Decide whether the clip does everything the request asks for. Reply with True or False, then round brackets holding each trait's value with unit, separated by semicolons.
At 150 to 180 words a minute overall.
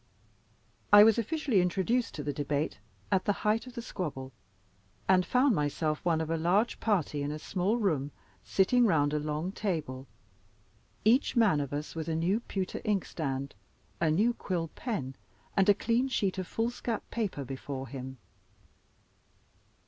True (155 wpm)